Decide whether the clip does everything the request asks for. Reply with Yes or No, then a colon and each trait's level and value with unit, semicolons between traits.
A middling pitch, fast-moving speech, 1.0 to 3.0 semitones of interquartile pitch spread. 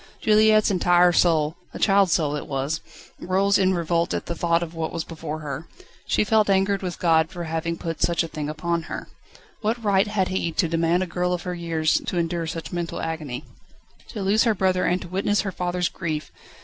Yes: medium, 175 Hz; fast, 210 wpm; average, 2.7 semitones